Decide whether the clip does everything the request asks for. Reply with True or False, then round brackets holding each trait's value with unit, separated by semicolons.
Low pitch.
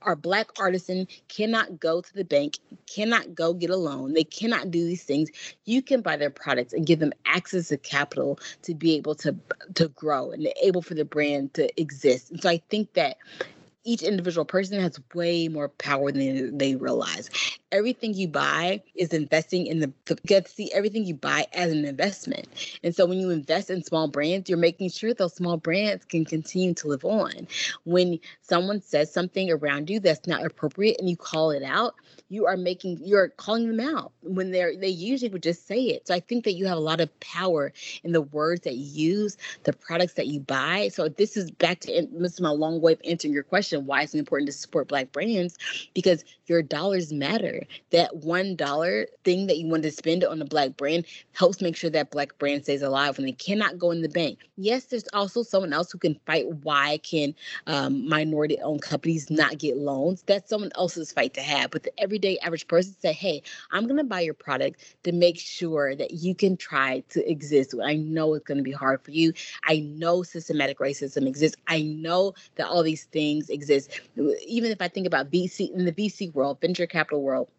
False (170 Hz)